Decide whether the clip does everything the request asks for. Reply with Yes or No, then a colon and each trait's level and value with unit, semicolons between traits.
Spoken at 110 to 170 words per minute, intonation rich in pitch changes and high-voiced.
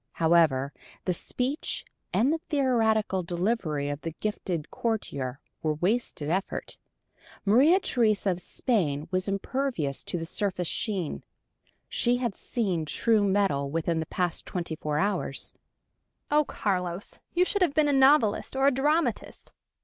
Yes: average, 140 wpm; wide, 6.9 semitones; high, 195 Hz